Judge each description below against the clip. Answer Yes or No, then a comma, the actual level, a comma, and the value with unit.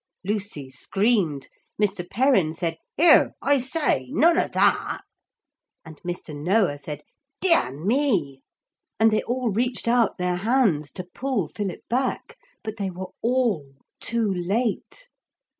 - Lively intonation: Yes, wide, 6.9 semitones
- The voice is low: No, high, 205 Hz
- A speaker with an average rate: No, slow, 130 wpm